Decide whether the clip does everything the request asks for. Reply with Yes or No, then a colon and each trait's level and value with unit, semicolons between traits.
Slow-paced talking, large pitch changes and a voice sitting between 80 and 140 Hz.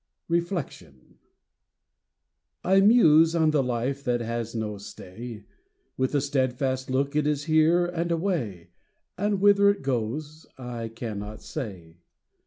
Yes: slow, 125 wpm; wide, 6.0 semitones; low, 135 Hz